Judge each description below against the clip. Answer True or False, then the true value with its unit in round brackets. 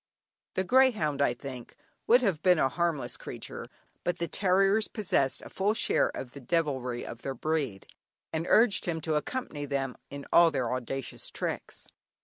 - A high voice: False (155 Hz)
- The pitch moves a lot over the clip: True (5.7 semitones)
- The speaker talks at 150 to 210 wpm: True (165 wpm)